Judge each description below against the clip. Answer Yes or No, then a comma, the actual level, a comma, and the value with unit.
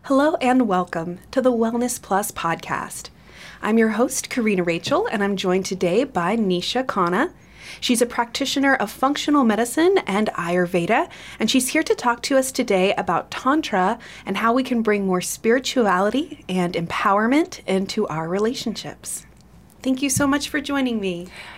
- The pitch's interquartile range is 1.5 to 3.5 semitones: No, wide, 5.6 semitones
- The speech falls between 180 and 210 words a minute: No, average, 160 wpm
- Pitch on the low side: No, high, 225 Hz